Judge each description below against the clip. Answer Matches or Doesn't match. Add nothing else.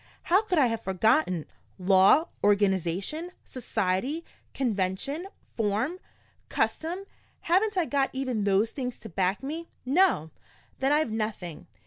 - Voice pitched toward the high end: Matches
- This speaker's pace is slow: Matches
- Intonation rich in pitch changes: Matches